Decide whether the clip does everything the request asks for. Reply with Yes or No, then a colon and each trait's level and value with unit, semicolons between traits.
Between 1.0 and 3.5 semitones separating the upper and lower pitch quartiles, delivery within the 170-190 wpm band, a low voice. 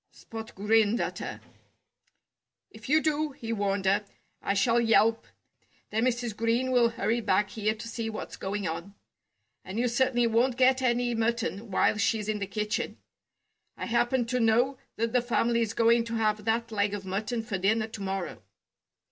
No: narrow, 2.4 semitones; average, 175 wpm; high, 225 Hz